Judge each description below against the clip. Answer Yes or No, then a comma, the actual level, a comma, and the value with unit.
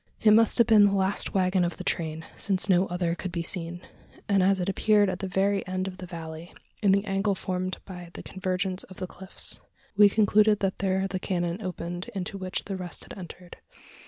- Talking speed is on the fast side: Yes, fast, 215 wpm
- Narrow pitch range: Yes, narrow, 1.8 semitones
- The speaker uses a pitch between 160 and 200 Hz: Yes, medium, 185 Hz